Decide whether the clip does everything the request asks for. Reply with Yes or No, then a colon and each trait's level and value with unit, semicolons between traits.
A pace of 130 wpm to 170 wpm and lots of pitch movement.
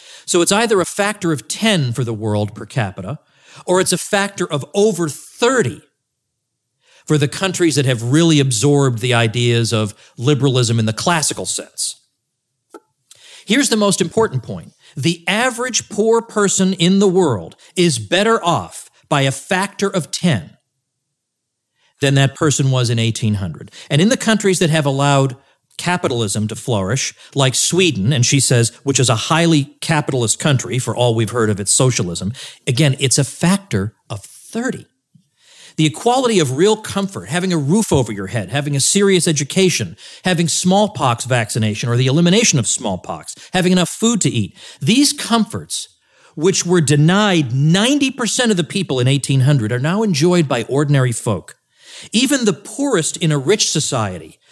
Yes: average, 160 wpm; wide, 6.8 semitones